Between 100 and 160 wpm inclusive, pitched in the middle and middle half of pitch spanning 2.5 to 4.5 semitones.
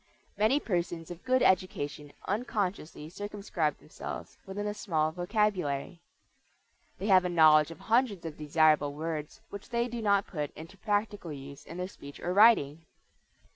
No: average, 150 wpm; medium, 180 Hz; average, 4.9 semitones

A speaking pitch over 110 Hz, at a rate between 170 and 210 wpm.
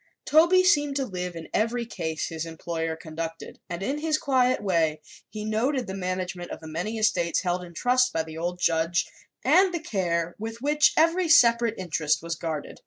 Yes: medium, 185 Hz; average, 185 wpm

